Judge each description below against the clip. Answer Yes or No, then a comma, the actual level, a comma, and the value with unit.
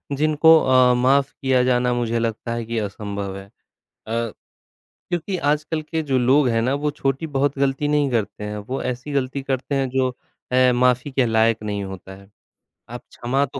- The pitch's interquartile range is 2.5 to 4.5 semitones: Yes, average, 3.4 semitones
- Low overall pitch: Yes, low, 130 Hz